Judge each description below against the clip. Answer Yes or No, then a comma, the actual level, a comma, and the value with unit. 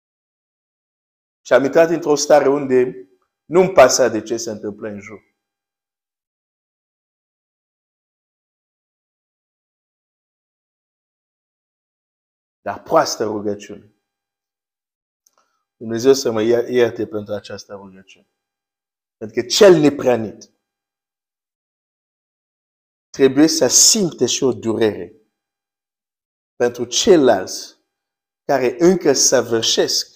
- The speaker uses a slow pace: Yes, slow, 80 wpm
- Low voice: Yes, low, 110 Hz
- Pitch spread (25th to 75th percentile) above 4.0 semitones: Yes, average, 5.0 semitones